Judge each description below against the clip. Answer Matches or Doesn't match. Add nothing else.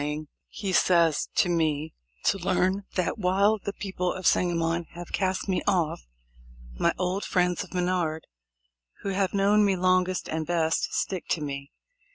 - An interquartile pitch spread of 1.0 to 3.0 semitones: Matches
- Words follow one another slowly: Doesn't match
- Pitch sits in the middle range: Matches